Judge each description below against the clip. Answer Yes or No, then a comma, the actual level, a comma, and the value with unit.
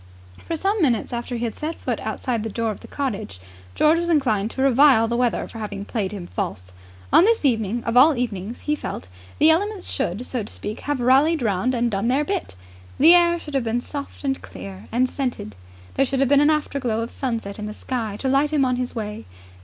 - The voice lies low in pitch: No, very high, 250 Hz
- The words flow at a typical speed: No, fast, 225 wpm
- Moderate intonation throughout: Yes, average, 4.9 semitones